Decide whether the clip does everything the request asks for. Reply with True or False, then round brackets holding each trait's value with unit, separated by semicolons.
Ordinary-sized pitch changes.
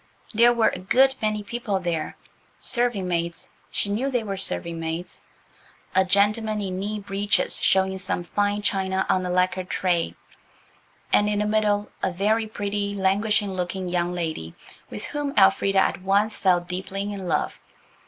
False (2.3 semitones)